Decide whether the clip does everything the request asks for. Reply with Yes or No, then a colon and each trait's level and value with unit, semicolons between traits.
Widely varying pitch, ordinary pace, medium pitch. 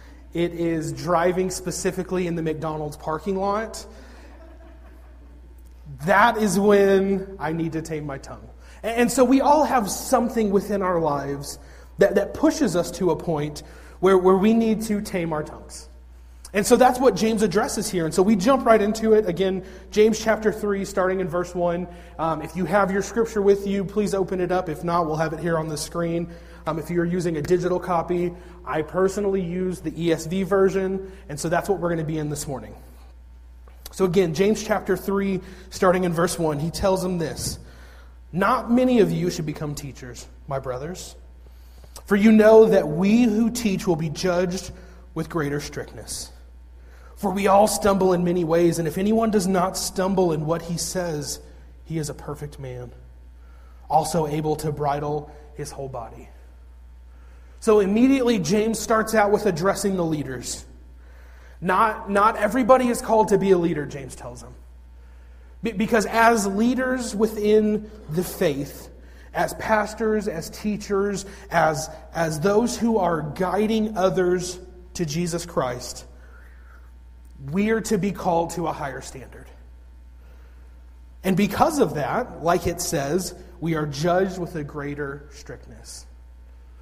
Yes: wide, 6.1 semitones; average, 160 wpm; medium, 175 Hz